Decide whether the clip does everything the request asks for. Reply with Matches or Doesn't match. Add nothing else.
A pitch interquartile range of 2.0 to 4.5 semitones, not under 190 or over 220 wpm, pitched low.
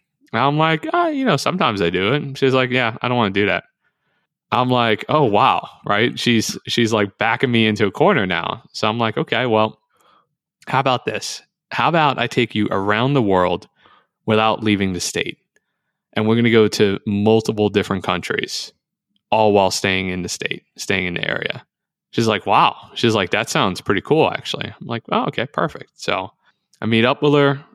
Matches